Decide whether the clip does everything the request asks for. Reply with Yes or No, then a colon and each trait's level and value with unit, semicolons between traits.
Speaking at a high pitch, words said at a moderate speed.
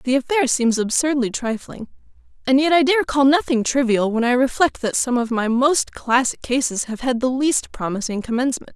Yes: very high, 255 Hz; average, 190 wpm